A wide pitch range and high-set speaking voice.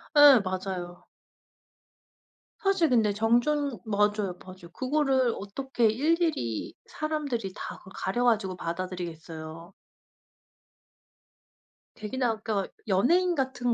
Yes: wide, 6.3 semitones; high, 220 Hz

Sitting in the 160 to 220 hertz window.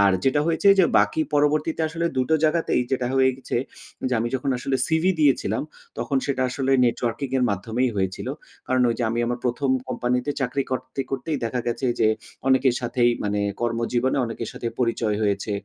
No: low, 130 Hz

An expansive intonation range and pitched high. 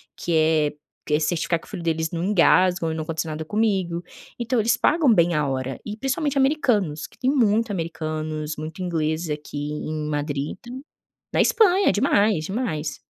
No: wide, 5.8 semitones; medium, 170 Hz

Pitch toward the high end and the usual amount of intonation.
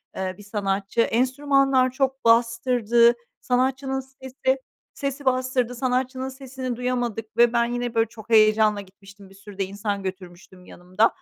Yes: high, 235 Hz; average, 4.0 semitones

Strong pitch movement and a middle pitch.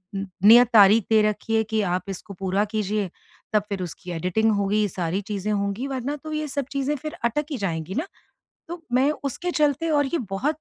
No: wide, 6.0 semitones; high, 215 Hz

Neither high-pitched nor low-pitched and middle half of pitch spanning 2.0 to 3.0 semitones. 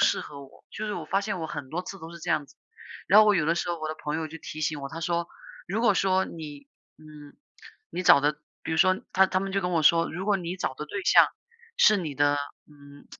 No: medium, 165 Hz; average, 3.9 semitones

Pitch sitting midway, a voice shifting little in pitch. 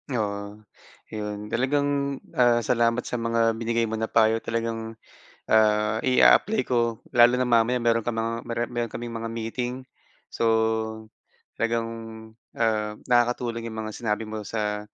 No: low, 115 Hz; narrow, 1.3 semitones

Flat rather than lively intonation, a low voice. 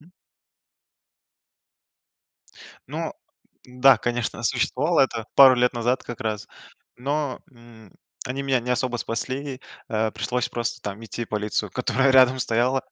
Yes: narrow, 2.3 semitones; low, 125 Hz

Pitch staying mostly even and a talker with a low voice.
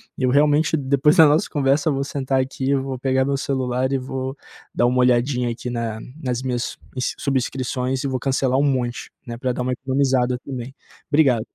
Yes: narrow, 1.6 semitones; low, 130 Hz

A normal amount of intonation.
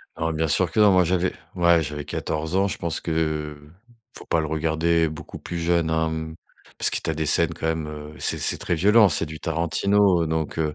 No: narrow, 1.7 semitones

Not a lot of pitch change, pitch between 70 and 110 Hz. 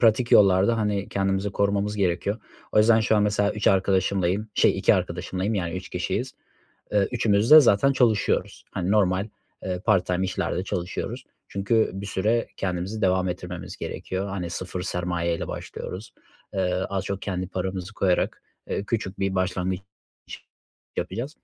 Yes: narrow, 2.2 semitones; very low, 95 Hz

